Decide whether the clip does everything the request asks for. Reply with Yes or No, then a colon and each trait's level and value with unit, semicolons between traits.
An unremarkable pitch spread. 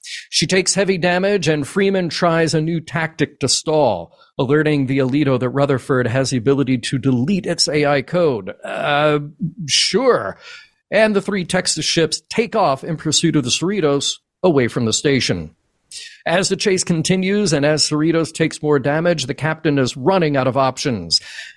Yes: average, 4.0 semitones